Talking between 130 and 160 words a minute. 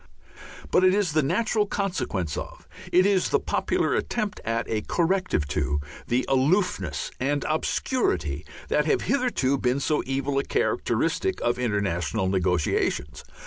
Yes: average, 140 wpm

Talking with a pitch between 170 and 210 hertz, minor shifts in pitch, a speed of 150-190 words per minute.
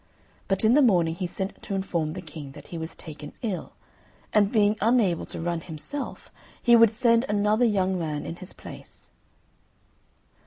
No: high, 190 Hz; average, 4.8 semitones; average, 170 wpm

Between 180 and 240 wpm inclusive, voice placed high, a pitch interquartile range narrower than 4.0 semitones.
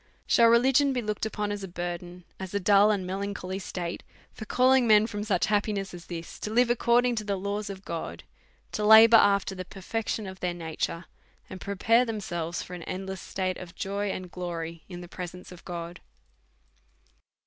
Yes: average, 190 wpm; high, 195 Hz; average, 3.1 semitones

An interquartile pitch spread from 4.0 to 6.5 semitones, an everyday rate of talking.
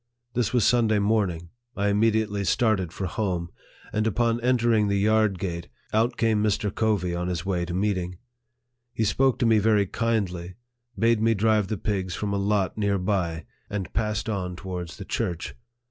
No: average, 3.2 semitones; average, 175 wpm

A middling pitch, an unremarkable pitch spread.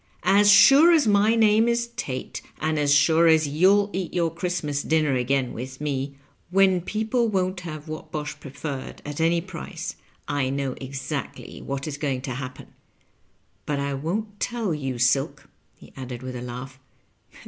No: medium, 155 Hz; wide, 5.9 semitones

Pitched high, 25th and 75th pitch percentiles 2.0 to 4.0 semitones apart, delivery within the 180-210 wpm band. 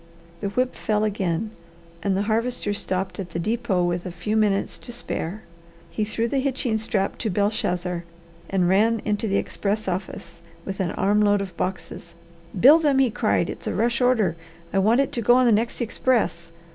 Yes: high, 210 Hz; average, 3.6 semitones; average, 190 wpm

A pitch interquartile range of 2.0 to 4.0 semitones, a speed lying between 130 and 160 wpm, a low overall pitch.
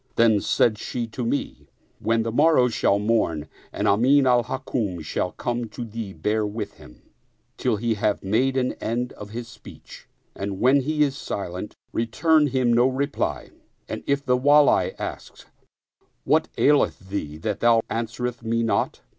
No: average, 3.5 semitones; average, 170 wpm; low, 115 Hz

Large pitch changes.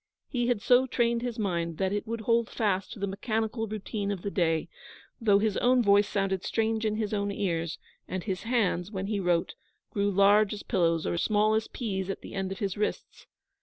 No: narrow, 2.5 semitones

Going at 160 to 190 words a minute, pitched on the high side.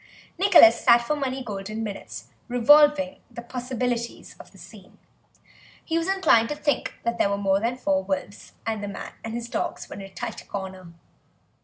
Yes: average, 185 wpm; high, 235 Hz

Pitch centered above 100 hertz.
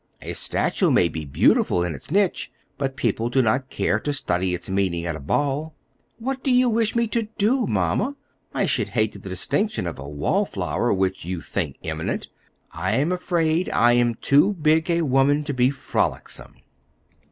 Yes: low, 135 Hz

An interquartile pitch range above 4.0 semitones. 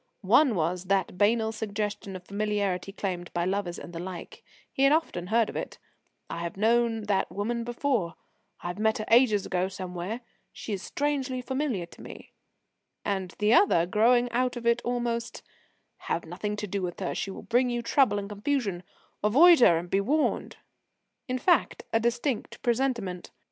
Yes: average, 4.5 semitones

